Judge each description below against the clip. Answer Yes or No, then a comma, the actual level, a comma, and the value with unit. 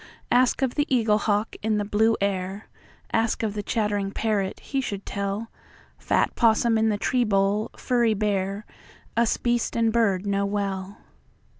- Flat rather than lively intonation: Yes, narrow, 2.3 semitones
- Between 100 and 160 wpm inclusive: Yes, average, 140 wpm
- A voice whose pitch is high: Yes, high, 210 Hz